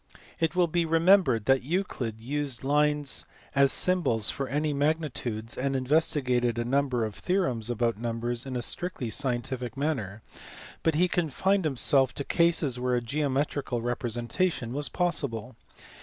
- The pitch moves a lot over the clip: No, average, 4.4 semitones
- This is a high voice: No, low, 135 Hz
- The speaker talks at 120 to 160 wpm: Yes, average, 145 wpm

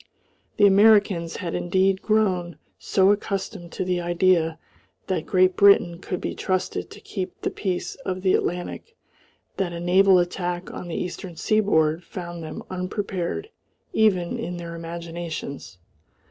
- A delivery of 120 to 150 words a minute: Yes, average, 140 wpm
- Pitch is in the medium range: Yes, medium, 180 Hz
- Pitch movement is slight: Yes, narrow, 2.1 semitones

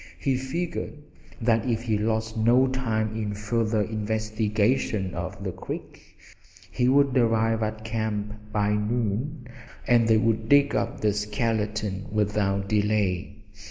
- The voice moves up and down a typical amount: No, narrow, 2.0 semitones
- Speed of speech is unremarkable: No, slow, 130 wpm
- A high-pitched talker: No, low, 110 Hz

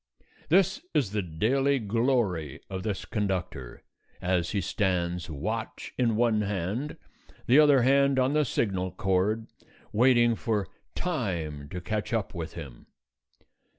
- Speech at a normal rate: No, slow, 130 wpm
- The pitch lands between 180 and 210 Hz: No, low, 105 Hz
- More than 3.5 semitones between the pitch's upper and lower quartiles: Yes, average, 5.2 semitones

